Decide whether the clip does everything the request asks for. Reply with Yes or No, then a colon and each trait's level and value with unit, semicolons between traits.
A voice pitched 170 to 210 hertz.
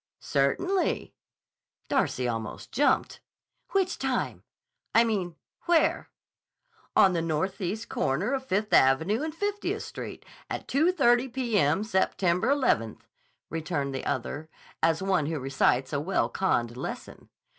Yes: high, 190 Hz